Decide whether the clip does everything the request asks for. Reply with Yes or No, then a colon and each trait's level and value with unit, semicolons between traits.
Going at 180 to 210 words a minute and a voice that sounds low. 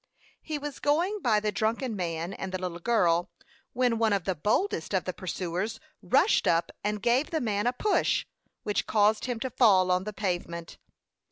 No: average, 185 wpm; high, 210 Hz